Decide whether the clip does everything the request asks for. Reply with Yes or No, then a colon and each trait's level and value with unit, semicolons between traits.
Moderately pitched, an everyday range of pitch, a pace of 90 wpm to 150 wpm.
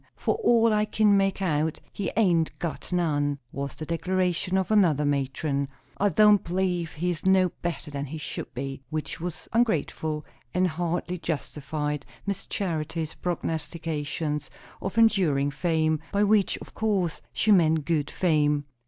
Yes: medium, 165 Hz; average, 4.1 semitones; average, 145 wpm